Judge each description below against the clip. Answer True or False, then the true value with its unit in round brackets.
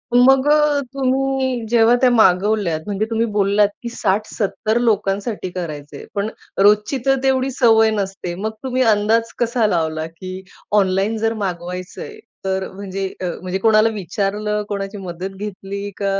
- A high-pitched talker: True (210 Hz)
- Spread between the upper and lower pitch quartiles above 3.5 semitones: False (3.2 semitones)